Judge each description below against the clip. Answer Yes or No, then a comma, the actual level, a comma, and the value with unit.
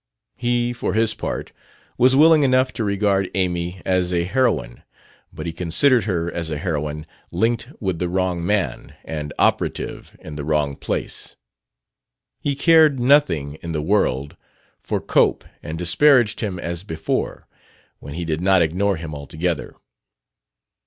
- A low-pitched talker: Yes, very low, 90 Hz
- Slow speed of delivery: No, average, 145 wpm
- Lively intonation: Yes, wide, 6.1 semitones